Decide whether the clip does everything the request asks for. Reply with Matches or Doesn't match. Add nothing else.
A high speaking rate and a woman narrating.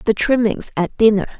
Doesn't match